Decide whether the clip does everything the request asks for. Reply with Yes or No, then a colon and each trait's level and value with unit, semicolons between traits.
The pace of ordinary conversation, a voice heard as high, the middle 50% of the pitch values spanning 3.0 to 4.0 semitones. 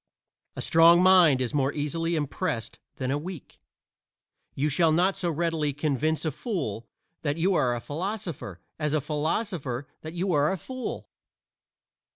No: average, 155 wpm; medium, 155 Hz; average, 3.5 semitones